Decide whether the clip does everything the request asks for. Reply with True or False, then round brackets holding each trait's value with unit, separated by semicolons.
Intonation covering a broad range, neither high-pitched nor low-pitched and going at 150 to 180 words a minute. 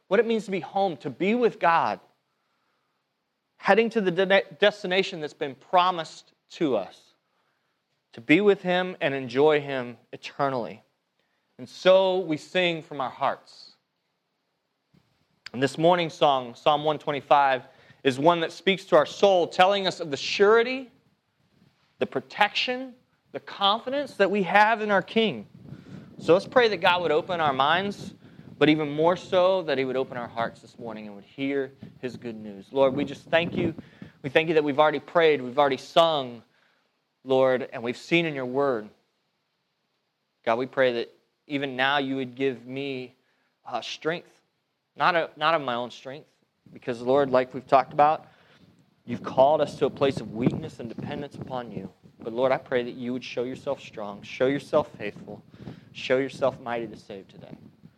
True (5.8 semitones; 150 Hz; 175 wpm)